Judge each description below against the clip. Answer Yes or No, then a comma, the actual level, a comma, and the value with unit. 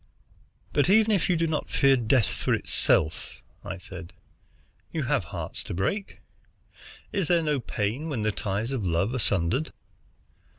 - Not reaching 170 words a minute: Yes, average, 160 wpm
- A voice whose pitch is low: Yes, low, 125 Hz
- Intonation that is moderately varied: No, wide, 8.3 semitones